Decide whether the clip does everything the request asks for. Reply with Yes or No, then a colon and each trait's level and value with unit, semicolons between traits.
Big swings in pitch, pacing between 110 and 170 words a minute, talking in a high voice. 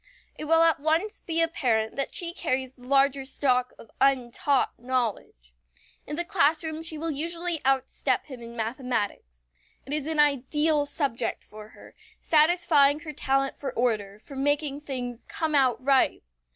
No: average, 3.9 semitones; average, 155 wpm; very high, 275 Hz